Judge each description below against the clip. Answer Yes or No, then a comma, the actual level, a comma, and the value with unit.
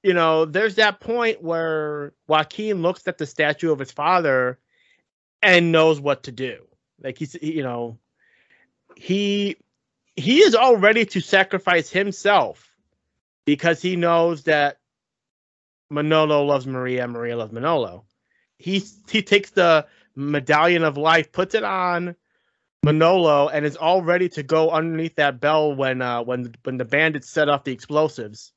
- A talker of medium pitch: Yes, medium, 160 Hz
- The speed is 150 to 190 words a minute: Yes, average, 155 wpm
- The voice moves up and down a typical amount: Yes, average, 4.1 semitones